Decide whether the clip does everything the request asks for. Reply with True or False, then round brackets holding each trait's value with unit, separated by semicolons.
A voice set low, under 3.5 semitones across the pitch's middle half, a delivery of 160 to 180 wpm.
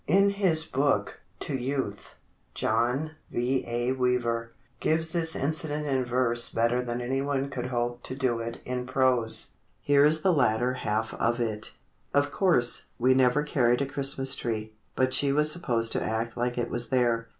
True (125 Hz; 3.0 semitones; 170 wpm)